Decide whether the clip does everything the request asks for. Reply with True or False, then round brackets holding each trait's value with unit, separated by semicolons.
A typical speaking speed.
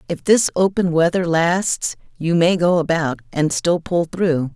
True (170 wpm)